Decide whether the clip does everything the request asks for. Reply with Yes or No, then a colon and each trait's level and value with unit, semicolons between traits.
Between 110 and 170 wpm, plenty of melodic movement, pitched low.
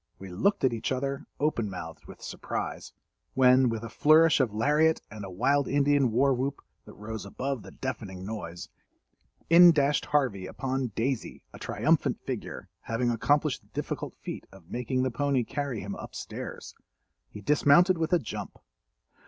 No: average, 160 wpm; average, 4.5 semitones; low, 130 Hz